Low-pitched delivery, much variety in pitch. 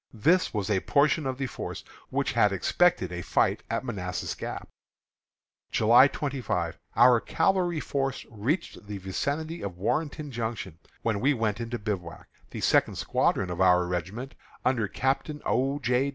Yes: low, 115 Hz; wide, 6.3 semitones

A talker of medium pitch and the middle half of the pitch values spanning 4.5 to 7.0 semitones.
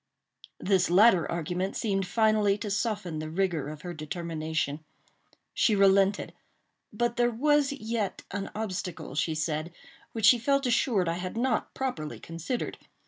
No: high, 195 Hz; average, 5.2 semitones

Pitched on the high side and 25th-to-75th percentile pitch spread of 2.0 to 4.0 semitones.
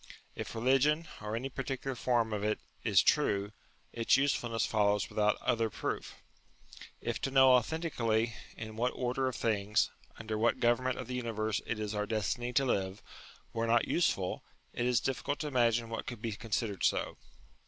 No: low, 115 Hz; average, 2.8 semitones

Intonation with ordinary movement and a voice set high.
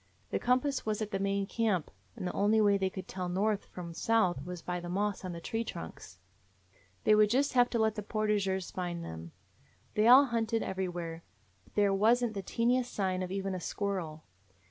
Yes: average, 3.4 semitones; high, 200 Hz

